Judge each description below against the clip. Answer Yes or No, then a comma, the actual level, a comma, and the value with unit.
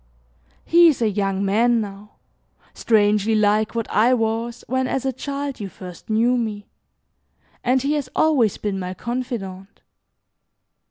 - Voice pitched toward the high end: Yes, high, 225 Hz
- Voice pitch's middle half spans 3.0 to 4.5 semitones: Yes, average, 3.6 semitones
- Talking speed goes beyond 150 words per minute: No, average, 145 wpm